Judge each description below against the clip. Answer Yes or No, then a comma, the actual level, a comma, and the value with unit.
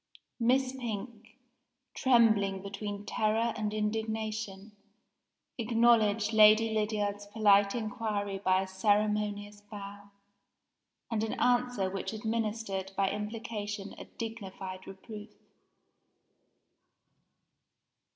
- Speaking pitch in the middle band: No, high, 210 Hz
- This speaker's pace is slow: Yes, slow, 85 wpm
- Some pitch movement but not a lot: No, narrow, 1.8 semitones